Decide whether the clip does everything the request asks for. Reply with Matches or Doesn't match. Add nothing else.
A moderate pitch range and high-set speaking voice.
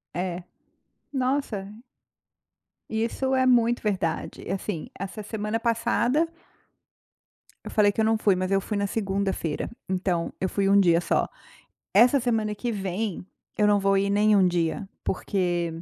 Matches